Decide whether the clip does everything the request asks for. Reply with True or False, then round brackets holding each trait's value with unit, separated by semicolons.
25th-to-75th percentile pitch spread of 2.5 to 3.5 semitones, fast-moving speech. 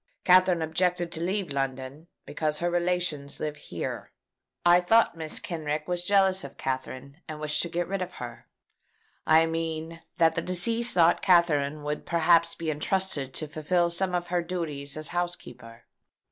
False (2.9 semitones; 160 wpm)